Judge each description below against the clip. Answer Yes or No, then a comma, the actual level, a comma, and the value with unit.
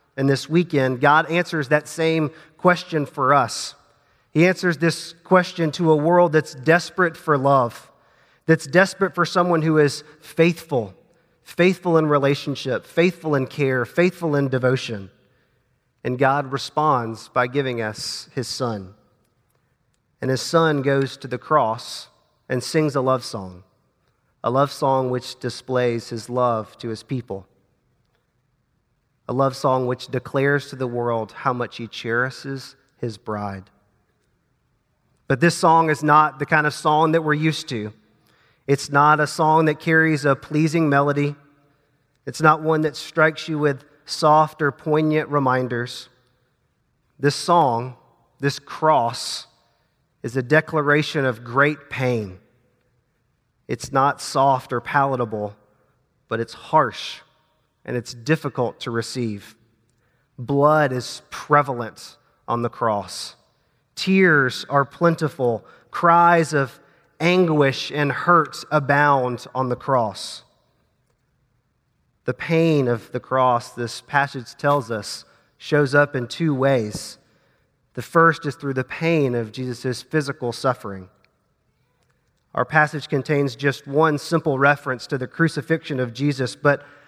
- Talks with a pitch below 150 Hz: Yes, medium, 140 Hz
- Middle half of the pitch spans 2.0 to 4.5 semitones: Yes, average, 3.6 semitones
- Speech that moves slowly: Yes, slow, 130 wpm